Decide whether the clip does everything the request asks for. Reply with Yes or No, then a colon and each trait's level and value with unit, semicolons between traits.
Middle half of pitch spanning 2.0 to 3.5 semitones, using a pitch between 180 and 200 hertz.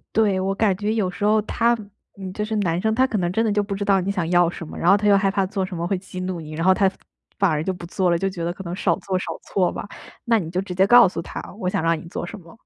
Yes: average, 2.7 semitones; high, 190 Hz